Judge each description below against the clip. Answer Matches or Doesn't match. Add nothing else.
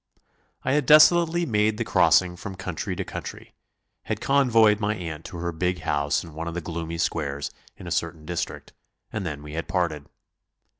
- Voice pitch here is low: Matches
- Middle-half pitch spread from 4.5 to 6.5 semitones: Matches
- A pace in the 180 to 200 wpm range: Matches